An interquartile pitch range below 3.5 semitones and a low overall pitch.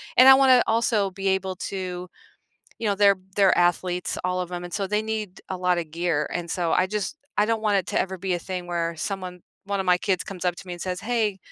No: narrow, 2.5 semitones; medium, 185 Hz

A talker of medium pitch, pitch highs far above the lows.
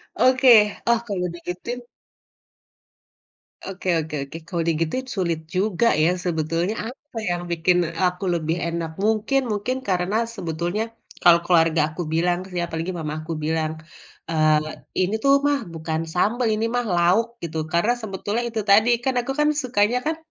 Yes: medium, 180 Hz; wide, 5.7 semitones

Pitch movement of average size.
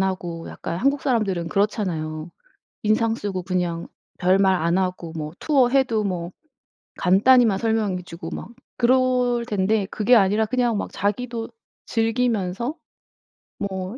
Yes: average, 4.5 semitones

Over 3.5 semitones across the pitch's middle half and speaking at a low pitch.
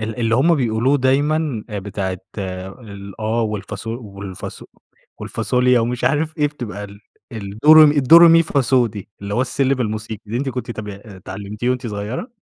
Yes: average, 4.5 semitones; low, 115 Hz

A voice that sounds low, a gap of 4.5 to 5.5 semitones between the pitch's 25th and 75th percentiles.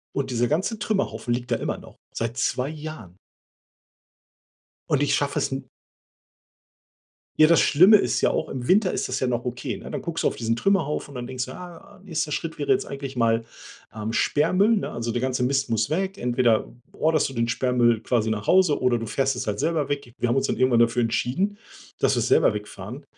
Yes: low, 130 Hz; average, 4.9 semitones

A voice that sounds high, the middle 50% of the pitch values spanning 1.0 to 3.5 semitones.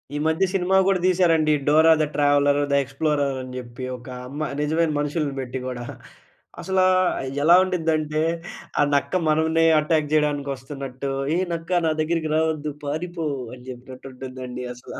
No: medium, 150 Hz; average, 3.1 semitones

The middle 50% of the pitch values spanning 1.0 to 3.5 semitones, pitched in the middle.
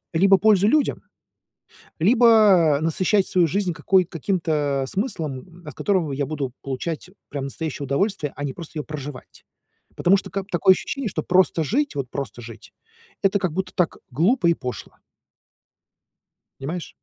No: average, 5.1 semitones; medium, 170 Hz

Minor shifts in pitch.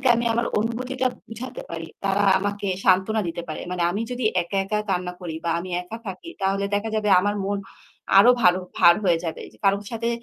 No: average, 3.8 semitones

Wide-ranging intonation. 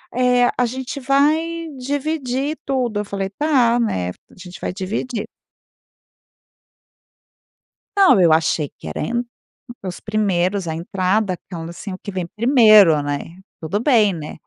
Yes: wide, 5.9 semitones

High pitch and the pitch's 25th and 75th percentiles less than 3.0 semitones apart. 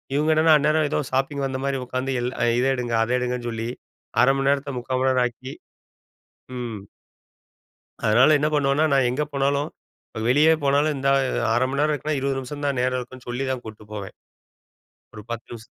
No: low, 130 Hz; narrow, 2.5 semitones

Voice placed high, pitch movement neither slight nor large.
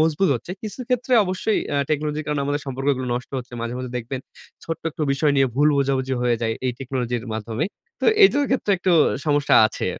No: medium, 140 Hz; average, 4.0 semitones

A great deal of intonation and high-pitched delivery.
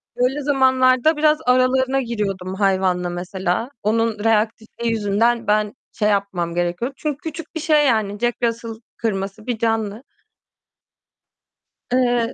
No: average, 4.2 semitones; high, 225 Hz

